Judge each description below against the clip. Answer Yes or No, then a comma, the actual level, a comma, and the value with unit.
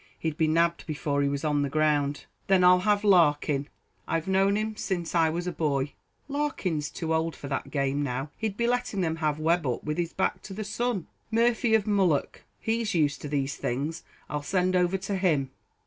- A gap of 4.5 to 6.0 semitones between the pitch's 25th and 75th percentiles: Yes, average, 4.8 semitones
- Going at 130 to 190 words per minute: No, fast, 205 wpm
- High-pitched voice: No, medium, 165 Hz